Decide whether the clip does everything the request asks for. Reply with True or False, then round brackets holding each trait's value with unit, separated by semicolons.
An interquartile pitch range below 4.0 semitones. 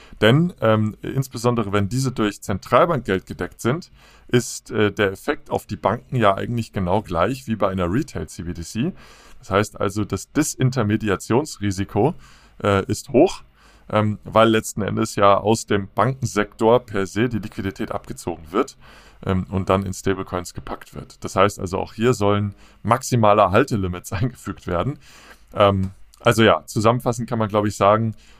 True (3.2 semitones)